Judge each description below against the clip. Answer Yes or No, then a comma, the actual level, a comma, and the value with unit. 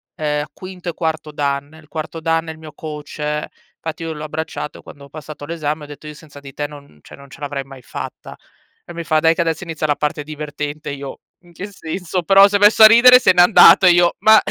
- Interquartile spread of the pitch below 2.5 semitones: No, average, 2.8 semitones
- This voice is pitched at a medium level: Yes, medium, 155 Hz